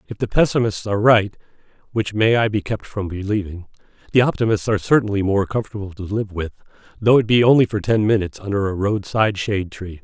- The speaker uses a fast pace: No, average, 185 wpm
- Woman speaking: No, male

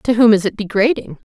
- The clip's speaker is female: Yes, female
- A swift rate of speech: Yes, fast, 230 wpm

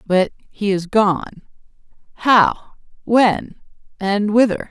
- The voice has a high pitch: Yes, high, 205 Hz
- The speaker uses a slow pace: Yes, slow, 65 wpm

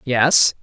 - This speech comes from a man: No, female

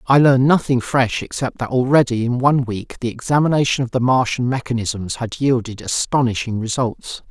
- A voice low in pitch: Yes, low, 125 Hz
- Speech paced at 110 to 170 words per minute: Yes, average, 165 wpm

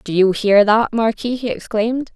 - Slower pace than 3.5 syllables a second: No, 4.9 syllables/s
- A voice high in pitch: Yes, high, 220 Hz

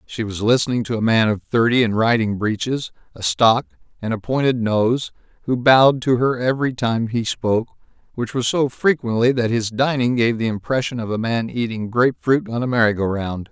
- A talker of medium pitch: No, low, 120 Hz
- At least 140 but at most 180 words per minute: No, fast, 205 wpm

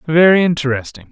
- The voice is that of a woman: No, male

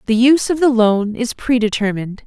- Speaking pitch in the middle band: No, high, 235 Hz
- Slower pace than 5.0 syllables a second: No, 5.8 syllables/s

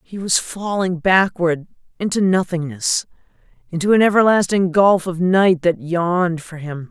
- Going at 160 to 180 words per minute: No, average, 140 wpm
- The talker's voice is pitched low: No, medium, 180 Hz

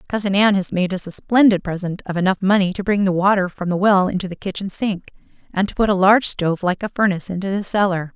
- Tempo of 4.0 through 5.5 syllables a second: No, 6.5 syllables/s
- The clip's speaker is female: Yes, female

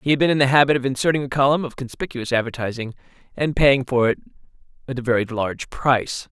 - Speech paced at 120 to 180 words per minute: No, average, 195 wpm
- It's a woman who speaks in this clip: No, male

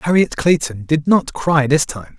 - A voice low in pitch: No, medium, 150 Hz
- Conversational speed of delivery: Yes, average, 190 wpm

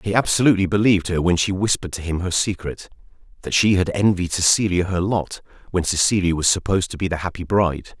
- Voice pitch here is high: No, very low, 90 Hz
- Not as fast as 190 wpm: No, average, 195 wpm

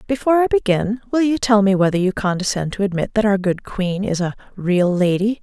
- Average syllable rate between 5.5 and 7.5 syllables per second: Yes, 5.7 syllables/s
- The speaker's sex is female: Yes, female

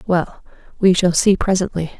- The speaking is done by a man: No, female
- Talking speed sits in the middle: Yes, average, 150 wpm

